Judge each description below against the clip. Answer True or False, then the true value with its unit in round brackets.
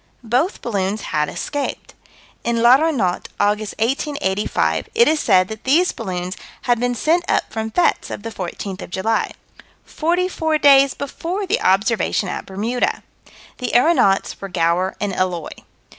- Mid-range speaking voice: False (225 Hz)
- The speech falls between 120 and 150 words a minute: True (145 wpm)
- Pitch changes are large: True (7.0 semitones)